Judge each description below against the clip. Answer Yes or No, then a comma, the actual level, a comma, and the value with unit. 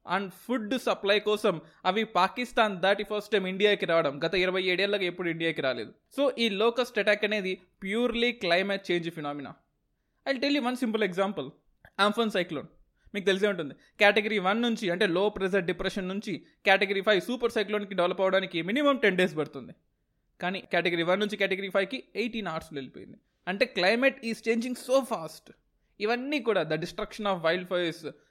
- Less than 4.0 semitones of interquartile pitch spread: Yes, average, 3.6 semitones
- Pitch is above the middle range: Yes, high, 200 Hz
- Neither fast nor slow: No, fast, 160 wpm